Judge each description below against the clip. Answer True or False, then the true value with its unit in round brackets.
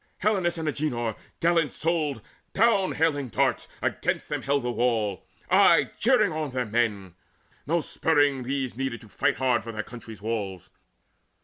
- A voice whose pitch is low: True (130 Hz)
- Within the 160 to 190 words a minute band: False (150 wpm)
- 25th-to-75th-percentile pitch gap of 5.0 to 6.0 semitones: True (5.4 semitones)